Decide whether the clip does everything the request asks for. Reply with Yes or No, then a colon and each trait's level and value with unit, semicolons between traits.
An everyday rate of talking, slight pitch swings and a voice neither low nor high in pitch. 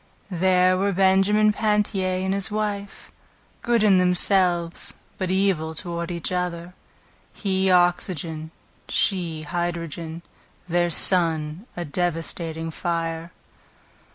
No: slow, 100 wpm; narrow, 2.3 semitones; medium, 180 Hz